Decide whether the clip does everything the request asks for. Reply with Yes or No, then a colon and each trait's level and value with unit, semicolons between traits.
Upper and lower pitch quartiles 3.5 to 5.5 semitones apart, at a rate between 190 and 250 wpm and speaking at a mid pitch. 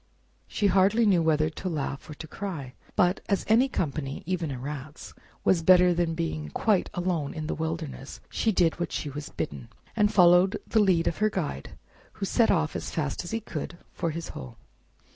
Yes: average, 3.9 semitones; average, 195 wpm; medium, 170 Hz